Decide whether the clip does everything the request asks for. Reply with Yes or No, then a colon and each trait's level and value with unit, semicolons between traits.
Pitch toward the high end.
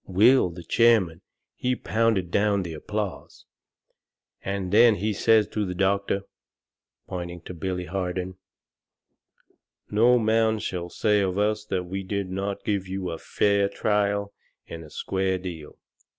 No: low, 100 Hz